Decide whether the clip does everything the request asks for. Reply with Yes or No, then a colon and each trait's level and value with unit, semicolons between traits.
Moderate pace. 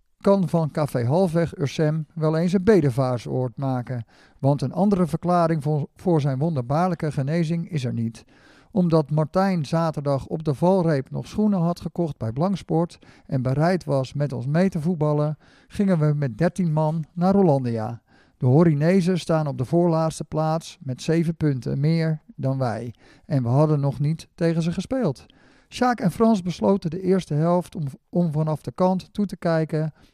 Yes: average, 170 wpm